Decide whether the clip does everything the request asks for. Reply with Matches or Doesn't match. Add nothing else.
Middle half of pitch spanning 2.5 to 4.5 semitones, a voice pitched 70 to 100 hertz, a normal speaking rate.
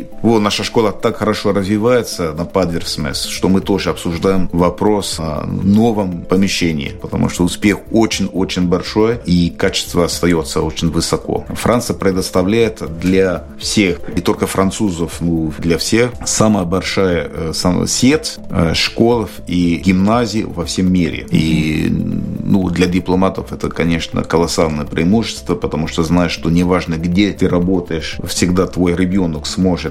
Matches